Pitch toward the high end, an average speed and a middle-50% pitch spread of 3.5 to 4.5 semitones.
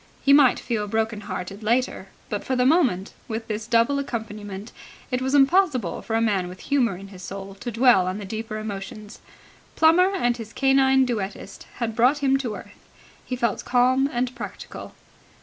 Yes: high, 230 Hz; average, 180 wpm; average, 4.1 semitones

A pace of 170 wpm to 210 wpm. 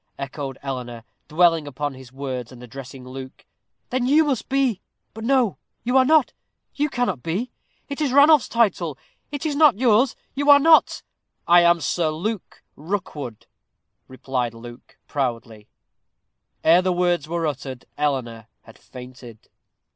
No: average, 145 wpm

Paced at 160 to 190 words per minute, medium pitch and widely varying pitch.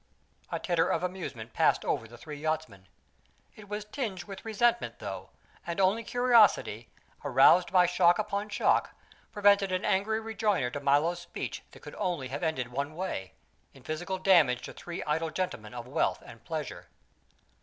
Yes: average, 165 wpm; medium, 175 Hz; wide, 5.9 semitones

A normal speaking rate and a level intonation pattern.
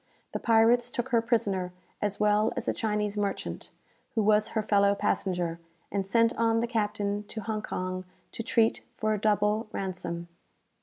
Yes: average, 165 wpm; narrow, 2.1 semitones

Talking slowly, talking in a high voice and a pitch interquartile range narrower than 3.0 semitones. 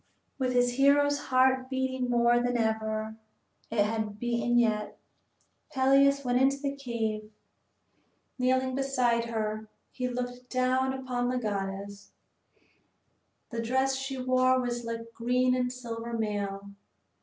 Yes: slow, 130 wpm; high, 245 Hz; narrow, 2.4 semitones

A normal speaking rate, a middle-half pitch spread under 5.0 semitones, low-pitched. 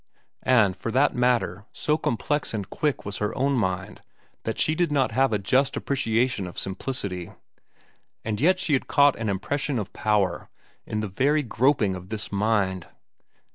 No: average, 170 wpm; average, 5.3 semitones; low, 115 Hz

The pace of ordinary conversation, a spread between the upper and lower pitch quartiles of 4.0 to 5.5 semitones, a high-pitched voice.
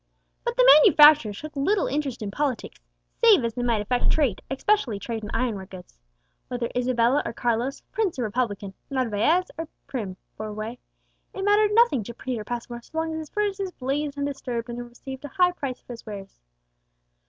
Yes: average, 185 wpm; average, 5.1 semitones; very high, 255 Hz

